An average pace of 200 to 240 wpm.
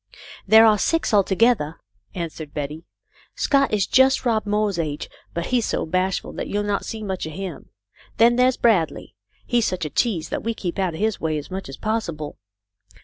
Yes: fast, 205 wpm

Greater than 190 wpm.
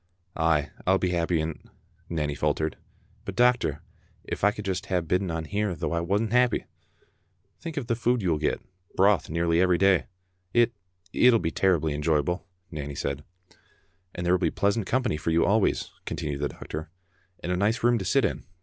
Yes: fast, 205 wpm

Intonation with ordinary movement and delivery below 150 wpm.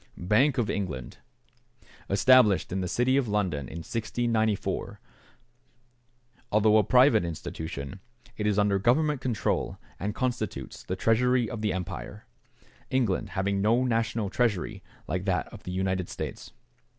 Yes: average, 4.3 semitones; slow, 135 wpm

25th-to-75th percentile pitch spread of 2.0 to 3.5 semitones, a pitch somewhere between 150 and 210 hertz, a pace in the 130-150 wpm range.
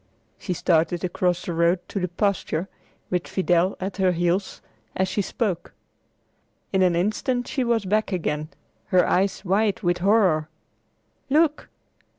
Yes: narrow, 2.6 semitones; medium, 185 Hz; average, 145 wpm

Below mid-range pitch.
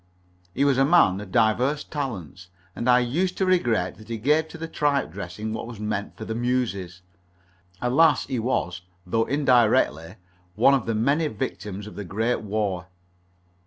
Yes: low, 115 Hz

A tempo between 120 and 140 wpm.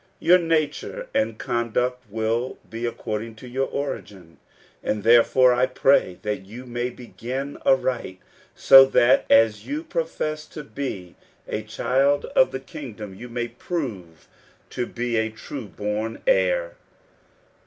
Yes: slow, 135 wpm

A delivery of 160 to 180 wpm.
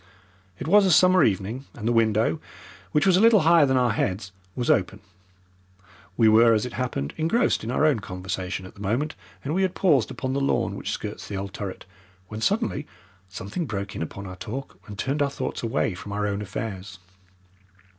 No: average, 200 wpm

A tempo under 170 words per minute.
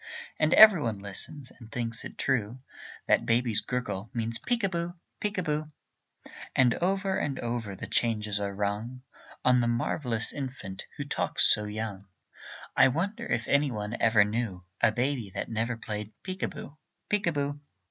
No: average, 175 wpm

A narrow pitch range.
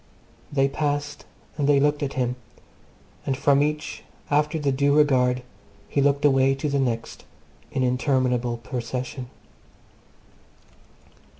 Yes: narrow, 2.3 semitones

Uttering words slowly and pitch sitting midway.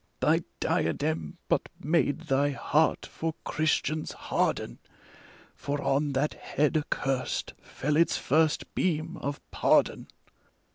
Yes: slow, 110 wpm; medium, 150 Hz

